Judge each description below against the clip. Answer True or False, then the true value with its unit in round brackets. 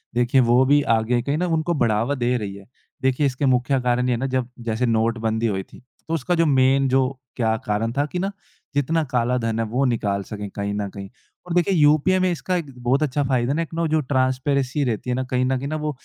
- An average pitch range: True (4.0 semitones)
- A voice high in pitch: False (130 Hz)